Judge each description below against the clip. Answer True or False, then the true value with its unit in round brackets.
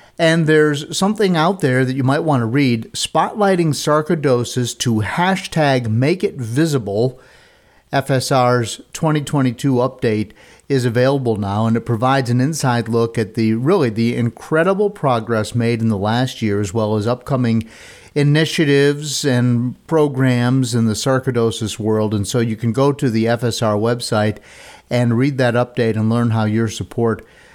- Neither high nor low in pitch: False (125 Hz)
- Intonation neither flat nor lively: True (3.9 semitones)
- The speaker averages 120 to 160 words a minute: True (150 wpm)